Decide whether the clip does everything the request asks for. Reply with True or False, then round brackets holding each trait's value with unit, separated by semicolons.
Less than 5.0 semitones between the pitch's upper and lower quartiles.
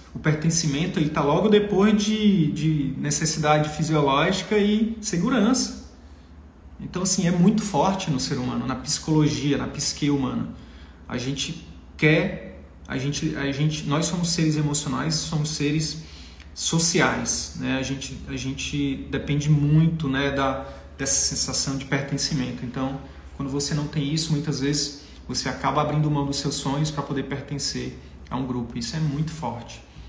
True (2.8 semitones)